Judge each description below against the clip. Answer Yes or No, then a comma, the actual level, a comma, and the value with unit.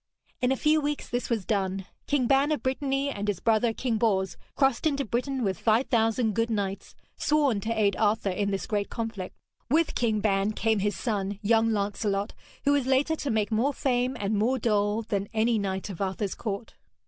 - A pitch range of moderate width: Yes, average, 4.0 semitones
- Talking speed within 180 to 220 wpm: Yes, average, 195 wpm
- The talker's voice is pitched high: Yes, high, 225 Hz